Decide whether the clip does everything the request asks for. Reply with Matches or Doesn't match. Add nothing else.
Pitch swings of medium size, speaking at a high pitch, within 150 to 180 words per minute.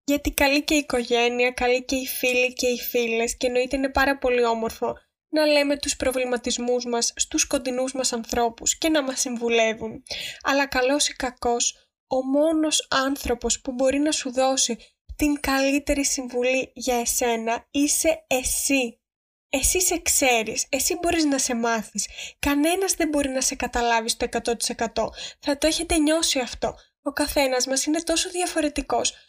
Matches